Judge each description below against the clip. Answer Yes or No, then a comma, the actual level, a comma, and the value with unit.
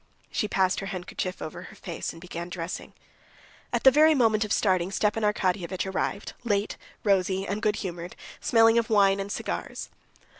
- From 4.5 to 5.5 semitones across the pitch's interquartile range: No, average, 2.7 semitones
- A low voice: No, high, 195 Hz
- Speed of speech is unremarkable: Yes, average, 165 wpm